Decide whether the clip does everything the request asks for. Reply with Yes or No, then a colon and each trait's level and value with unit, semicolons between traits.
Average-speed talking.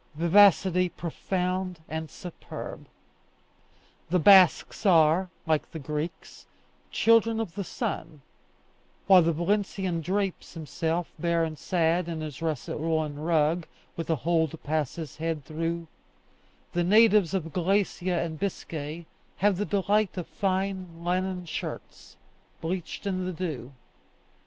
No: slow, 130 wpm